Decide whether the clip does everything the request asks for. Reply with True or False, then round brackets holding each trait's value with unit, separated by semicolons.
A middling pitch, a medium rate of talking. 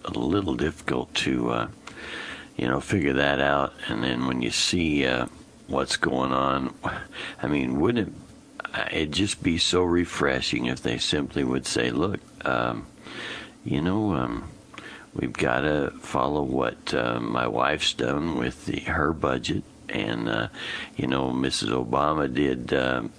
False (65 Hz; 155 wpm)